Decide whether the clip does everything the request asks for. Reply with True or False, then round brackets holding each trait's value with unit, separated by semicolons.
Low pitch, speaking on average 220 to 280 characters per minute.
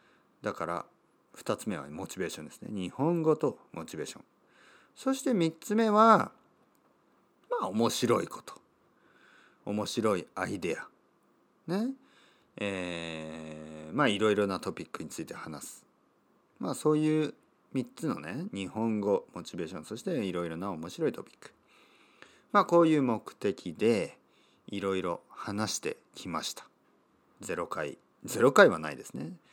True (110 Hz; 260 characters per minute)